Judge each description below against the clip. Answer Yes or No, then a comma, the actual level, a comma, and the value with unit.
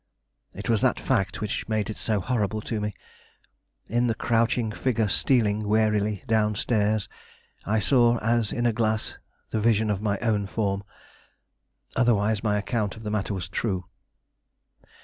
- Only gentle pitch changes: Yes, narrow, 1.8 semitones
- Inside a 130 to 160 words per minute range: Yes, average, 155 wpm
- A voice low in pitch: Yes, low, 110 Hz